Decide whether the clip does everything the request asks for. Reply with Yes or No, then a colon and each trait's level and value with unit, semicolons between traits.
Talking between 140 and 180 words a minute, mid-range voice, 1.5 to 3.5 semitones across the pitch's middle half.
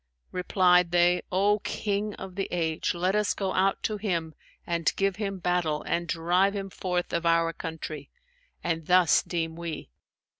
Yes: average, 160 wpm; medium, 180 Hz; narrow, 2.6 semitones